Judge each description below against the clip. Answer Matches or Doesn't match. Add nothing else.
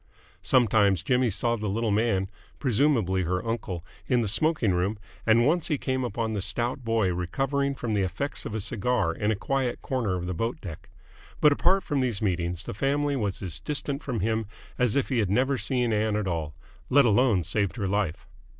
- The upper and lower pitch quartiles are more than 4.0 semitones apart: Matches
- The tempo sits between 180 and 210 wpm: Matches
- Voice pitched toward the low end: Matches